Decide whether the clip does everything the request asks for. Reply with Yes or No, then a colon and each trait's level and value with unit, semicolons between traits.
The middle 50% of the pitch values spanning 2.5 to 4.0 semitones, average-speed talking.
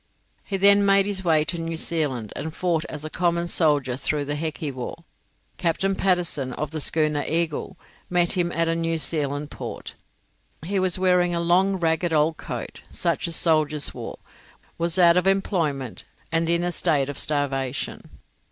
Yes: average, 2.9 semitones; average, 170 wpm